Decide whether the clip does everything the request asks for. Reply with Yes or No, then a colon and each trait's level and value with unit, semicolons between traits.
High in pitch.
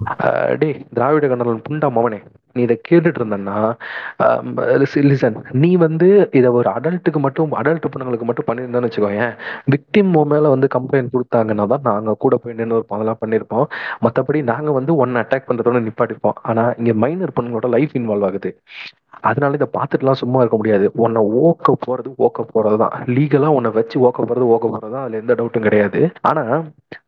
No: low, 125 Hz